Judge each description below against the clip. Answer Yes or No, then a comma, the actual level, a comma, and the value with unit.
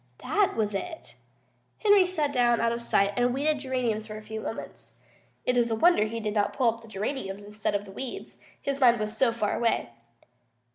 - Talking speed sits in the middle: Yes, average, 195 wpm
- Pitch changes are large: No, average, 3.8 semitones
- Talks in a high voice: Yes, high, 230 Hz